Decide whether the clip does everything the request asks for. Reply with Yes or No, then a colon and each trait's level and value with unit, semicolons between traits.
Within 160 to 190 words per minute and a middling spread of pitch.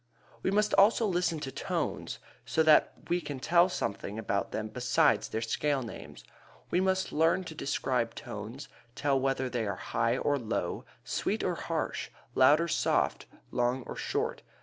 No: average, 165 wpm; wide, 6.0 semitones